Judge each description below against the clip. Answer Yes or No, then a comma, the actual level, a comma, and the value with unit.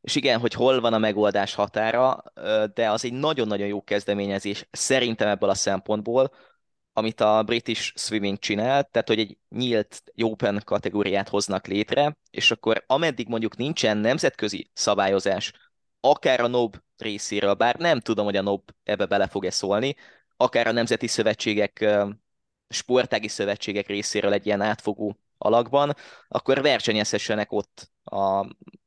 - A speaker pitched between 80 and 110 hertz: Yes, low, 105 Hz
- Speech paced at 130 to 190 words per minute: Yes, average, 140 wpm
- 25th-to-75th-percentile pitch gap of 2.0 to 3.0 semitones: Yes, narrow, 2.6 semitones